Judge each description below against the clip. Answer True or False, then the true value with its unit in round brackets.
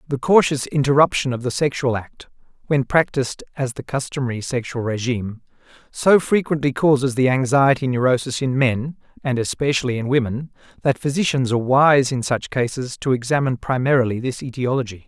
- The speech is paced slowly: False (150 wpm)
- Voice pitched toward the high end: False (130 Hz)